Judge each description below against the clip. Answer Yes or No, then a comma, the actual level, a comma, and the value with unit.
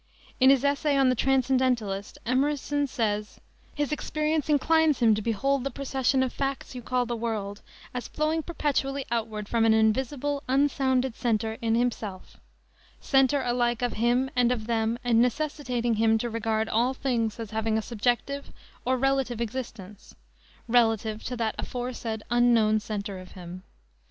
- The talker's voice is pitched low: No, high, 245 Hz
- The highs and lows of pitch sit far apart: No, average, 3.4 semitones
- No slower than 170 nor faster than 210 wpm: No, average, 155 wpm